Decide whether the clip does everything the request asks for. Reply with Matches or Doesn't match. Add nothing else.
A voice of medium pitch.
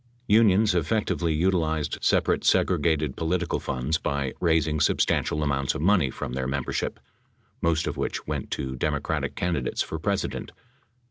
Doesn't match